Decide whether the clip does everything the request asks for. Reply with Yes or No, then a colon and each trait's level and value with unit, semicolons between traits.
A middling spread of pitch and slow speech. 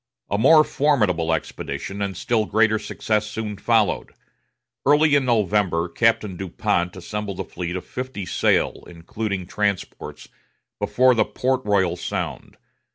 Yes: average, 4.0 semitones; slow, 130 wpm